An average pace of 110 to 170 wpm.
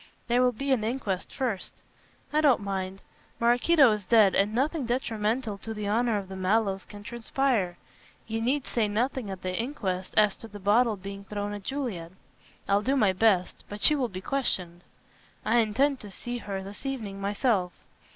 No: average, 180 wpm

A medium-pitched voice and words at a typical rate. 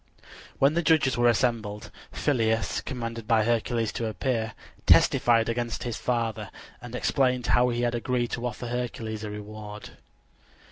No: low, 120 Hz; average, 145 wpm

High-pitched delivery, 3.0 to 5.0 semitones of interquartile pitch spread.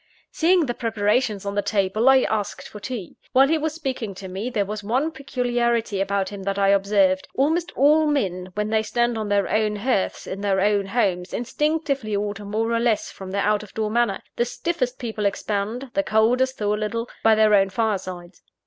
Yes: high, 215 Hz; average, 3.8 semitones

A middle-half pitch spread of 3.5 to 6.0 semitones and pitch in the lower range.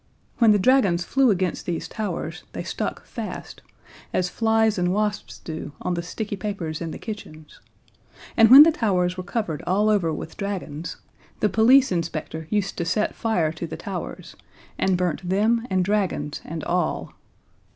No: average, 4.2 semitones; medium, 185 Hz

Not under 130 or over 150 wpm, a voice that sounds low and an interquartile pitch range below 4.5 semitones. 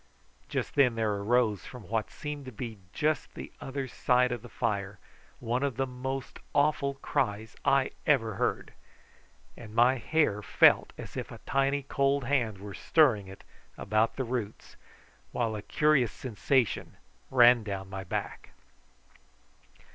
Yes: average, 145 wpm; low, 120 Hz; average, 4.1 semitones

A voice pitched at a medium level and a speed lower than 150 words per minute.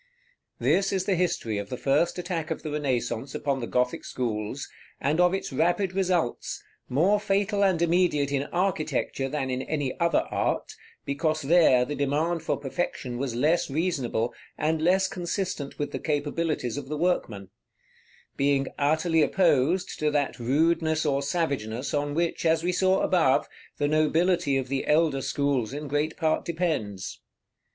No: medium, 150 Hz; average, 160 wpm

